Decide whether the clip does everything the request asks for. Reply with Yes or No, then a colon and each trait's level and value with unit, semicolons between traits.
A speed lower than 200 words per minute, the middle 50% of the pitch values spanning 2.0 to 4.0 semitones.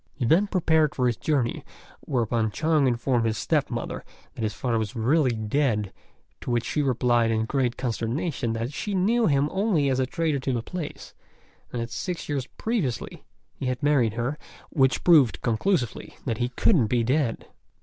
No: average, 180 wpm; average, 4.6 semitones